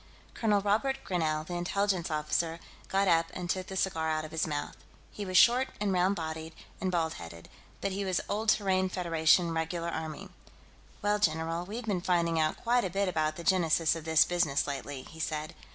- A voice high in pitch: No, medium, 170 Hz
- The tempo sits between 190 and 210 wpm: Yes, average, 195 wpm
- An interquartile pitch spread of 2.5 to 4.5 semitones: Yes, average, 3.3 semitones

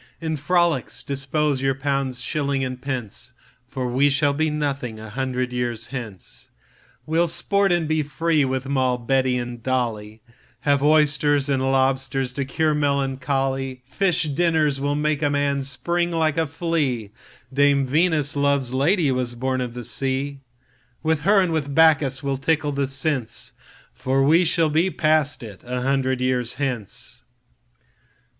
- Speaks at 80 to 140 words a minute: Yes, slow, 135 wpm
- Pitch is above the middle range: No, low, 135 Hz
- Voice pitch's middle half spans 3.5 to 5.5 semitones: No, average, 2.9 semitones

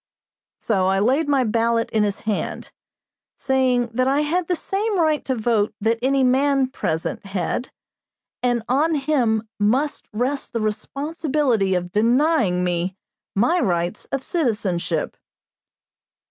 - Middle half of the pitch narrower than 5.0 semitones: No, average, 5.3 semitones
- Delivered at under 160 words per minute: Yes, slow, 135 wpm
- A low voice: No, high, 245 Hz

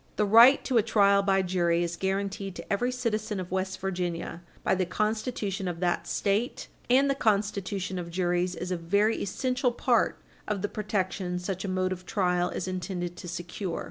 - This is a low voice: No, high, 190 Hz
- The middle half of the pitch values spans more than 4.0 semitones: No, average, 2.8 semitones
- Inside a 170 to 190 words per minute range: Yes, average, 185 wpm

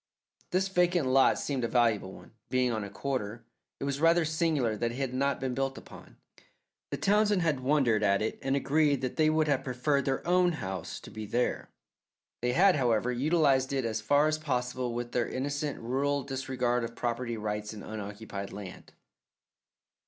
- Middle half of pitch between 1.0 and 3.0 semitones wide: No, average, 3.9 semitones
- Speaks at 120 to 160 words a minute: No, average, 180 wpm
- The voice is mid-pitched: No, low, 130 Hz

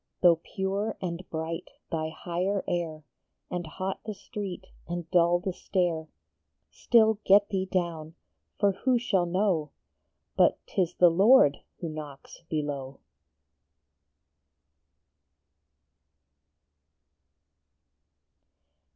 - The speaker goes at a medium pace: No, slow, 100 wpm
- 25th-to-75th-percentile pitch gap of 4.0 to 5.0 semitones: No, average, 3.3 semitones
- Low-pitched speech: No, medium, 175 Hz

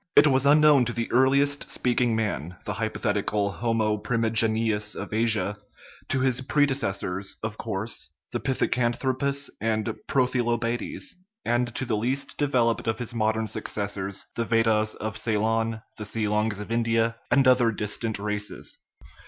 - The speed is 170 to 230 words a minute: No, average, 145 wpm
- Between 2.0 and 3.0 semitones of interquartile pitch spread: Yes, narrow, 2.6 semitones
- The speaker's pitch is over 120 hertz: No, low, 115 Hz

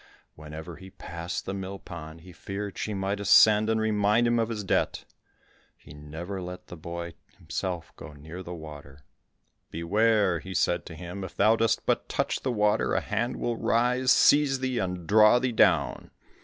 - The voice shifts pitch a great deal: No, average, 4.4 semitones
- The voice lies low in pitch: Yes, very low, 95 Hz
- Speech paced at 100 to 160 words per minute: No, average, 180 wpm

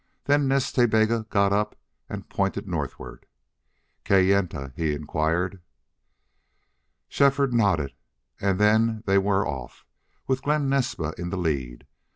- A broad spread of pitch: Yes, wide, 6.3 semitones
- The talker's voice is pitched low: Yes, low, 100 Hz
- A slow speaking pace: Yes, slow, 125 wpm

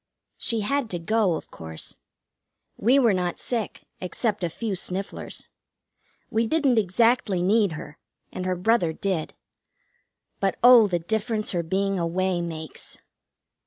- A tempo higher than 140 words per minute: No, slow, 135 wpm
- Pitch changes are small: No, average, 4.4 semitones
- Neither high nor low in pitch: No, high, 195 Hz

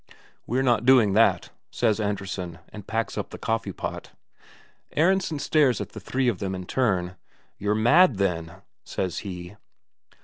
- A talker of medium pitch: No, low, 105 Hz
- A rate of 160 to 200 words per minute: No, average, 150 wpm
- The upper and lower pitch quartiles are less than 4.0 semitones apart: No, average, 4.8 semitones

